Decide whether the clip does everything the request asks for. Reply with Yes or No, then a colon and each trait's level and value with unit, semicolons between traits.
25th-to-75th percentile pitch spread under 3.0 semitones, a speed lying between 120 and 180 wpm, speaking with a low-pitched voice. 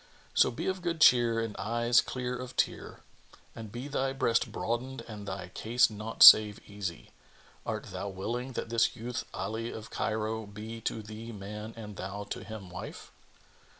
Yes: narrow, 2.4 semitones; average, 170 wpm; low, 115 Hz